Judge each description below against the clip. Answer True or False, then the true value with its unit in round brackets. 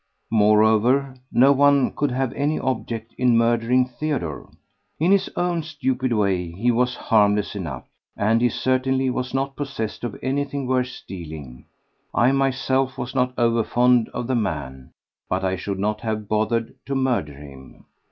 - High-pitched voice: False (120 Hz)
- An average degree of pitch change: True (4.0 semitones)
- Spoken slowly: False (150 wpm)